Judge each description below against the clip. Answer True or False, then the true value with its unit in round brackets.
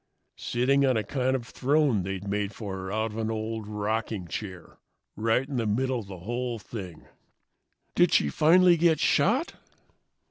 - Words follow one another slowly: False (170 wpm)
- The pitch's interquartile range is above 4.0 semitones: True (4.4 semitones)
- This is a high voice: False (110 Hz)